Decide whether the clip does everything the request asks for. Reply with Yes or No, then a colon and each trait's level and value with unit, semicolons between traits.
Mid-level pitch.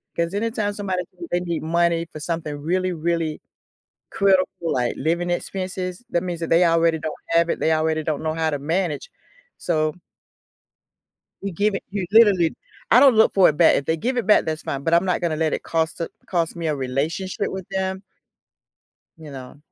Yes: medium, 170 Hz